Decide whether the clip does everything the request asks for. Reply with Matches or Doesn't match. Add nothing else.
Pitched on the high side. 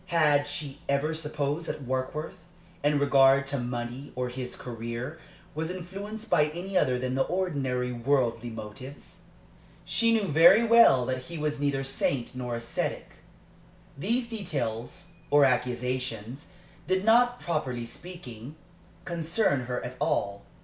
Doesn't match